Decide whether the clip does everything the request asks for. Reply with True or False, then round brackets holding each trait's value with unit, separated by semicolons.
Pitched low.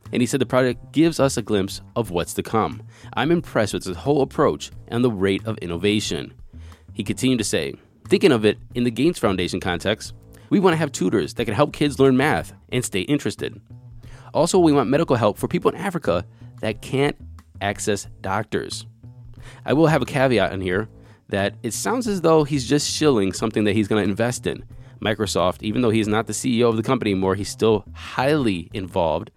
True (110 Hz)